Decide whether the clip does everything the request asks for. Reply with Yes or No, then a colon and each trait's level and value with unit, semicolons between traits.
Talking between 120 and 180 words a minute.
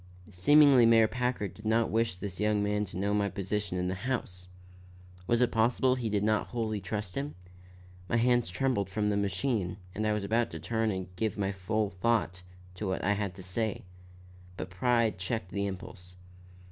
No: average, 190 wpm